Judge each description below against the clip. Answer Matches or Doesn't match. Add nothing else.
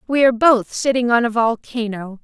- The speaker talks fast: Doesn't match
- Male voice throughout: Doesn't match